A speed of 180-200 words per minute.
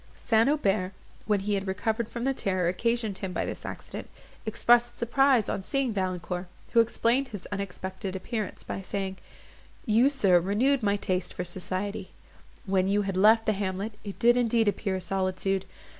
No: average, 170 wpm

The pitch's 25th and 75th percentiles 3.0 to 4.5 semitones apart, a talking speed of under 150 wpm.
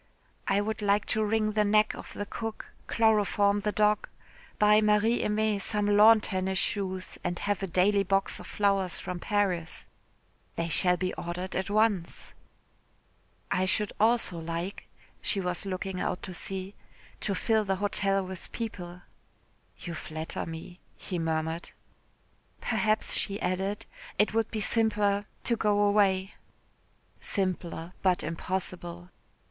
No: narrow, 2.6 semitones; average, 140 wpm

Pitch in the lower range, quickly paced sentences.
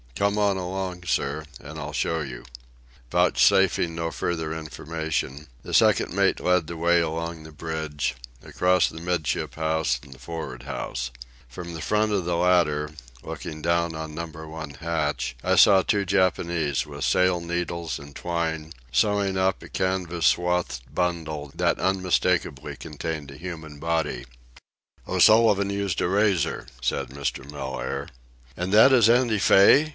No: very low, 85 Hz; average, 150 wpm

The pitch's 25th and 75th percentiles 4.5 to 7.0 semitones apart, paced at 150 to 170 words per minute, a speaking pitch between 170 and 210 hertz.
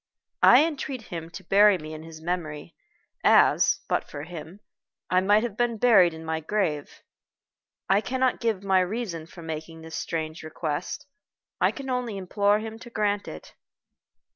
Yes: average, 5.1 semitones; average, 165 wpm; medium, 185 Hz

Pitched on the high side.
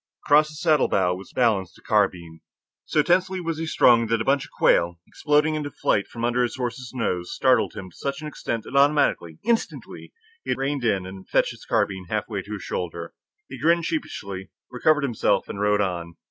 No: low, 120 Hz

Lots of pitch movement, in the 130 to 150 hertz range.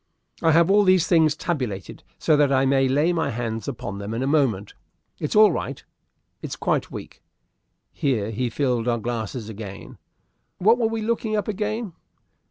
Yes: wide, 8.2 semitones; medium, 140 Hz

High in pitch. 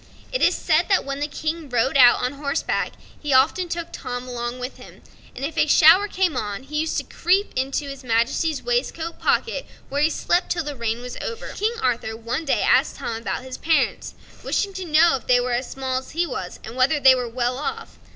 Yes: very high, 275 Hz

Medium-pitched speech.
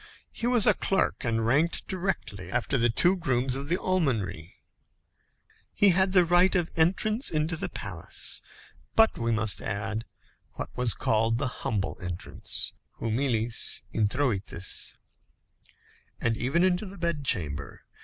No: low, 130 Hz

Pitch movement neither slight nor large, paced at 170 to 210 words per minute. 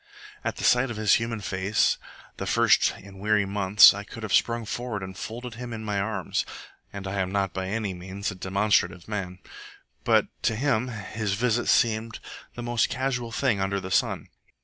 Yes: average, 3.0 semitones; average, 190 wpm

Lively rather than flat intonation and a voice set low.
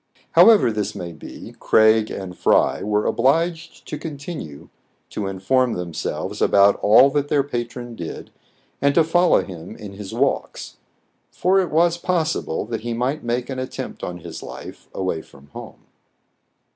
Yes: wide, 7.3 semitones; low, 120 Hz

